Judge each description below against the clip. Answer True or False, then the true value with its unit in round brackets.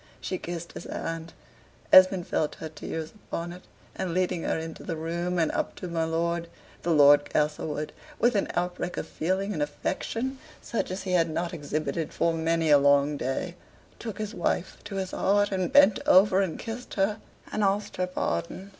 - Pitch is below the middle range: False (175 Hz)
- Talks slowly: False (185 wpm)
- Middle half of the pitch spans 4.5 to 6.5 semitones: False (3.1 semitones)